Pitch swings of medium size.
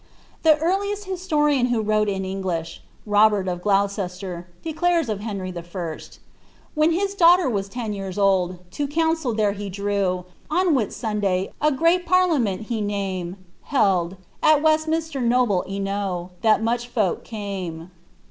No: wide, 8.0 semitones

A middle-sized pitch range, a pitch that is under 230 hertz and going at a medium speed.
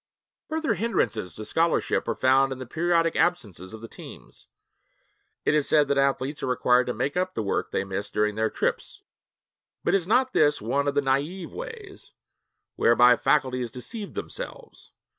No: wide, 6.6 semitones; medium, 140 Hz; average, 170 wpm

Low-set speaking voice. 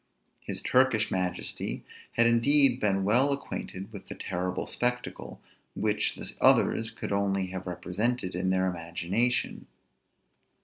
Yes: low, 100 Hz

